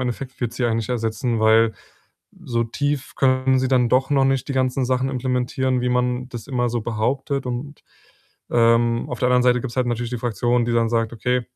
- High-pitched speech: No, low, 125 Hz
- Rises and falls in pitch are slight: Yes, narrow, 1.8 semitones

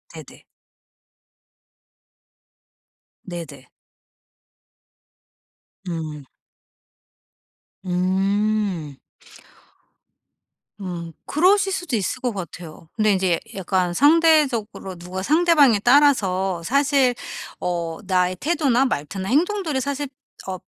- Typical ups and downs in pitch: No, wide, 7.9 semitones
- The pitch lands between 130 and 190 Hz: No, high, 200 Hz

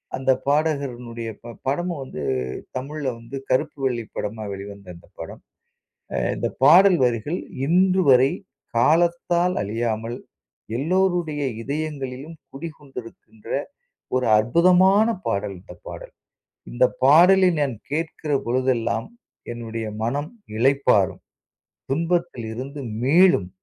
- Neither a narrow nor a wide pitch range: No, wide, 6.2 semitones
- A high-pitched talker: No, low, 135 Hz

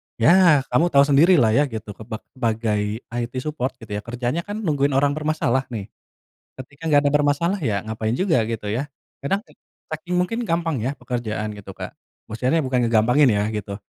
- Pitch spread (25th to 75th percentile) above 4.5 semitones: Yes, wide, 5.5 semitones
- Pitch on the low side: Yes, low, 130 Hz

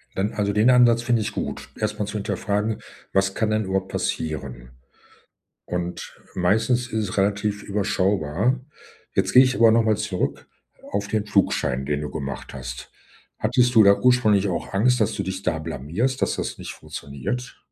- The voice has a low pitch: Yes, low, 100 Hz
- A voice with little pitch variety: No, average, 3.7 semitones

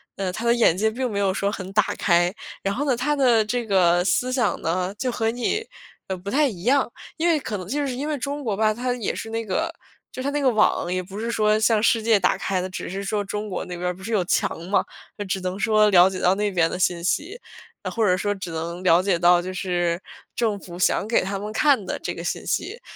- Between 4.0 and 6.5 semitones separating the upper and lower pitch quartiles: Yes, average, 4.4 semitones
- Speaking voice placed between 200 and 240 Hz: Yes, high, 205 Hz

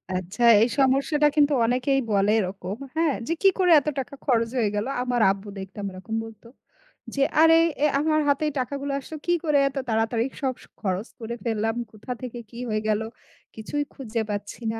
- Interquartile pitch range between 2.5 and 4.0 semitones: No, average, 4.7 semitones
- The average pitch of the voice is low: No, high, 240 Hz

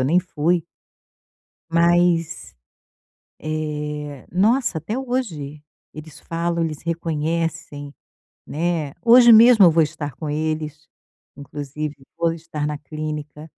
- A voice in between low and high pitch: Yes, medium, 160 Hz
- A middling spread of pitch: No, narrow, 2.3 semitones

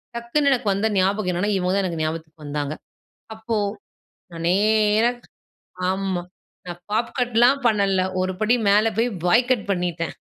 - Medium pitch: No, high, 200 Hz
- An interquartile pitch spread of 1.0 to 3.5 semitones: No, average, 4.2 semitones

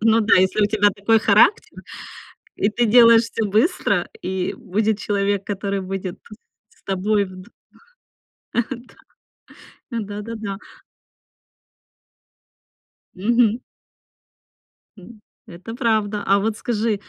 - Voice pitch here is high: Yes, high, 210 Hz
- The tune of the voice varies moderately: No, narrow, 2.3 semitones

